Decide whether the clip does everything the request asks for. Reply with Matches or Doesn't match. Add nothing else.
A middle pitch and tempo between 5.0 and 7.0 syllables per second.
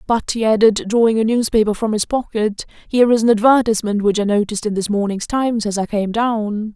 Doesn't match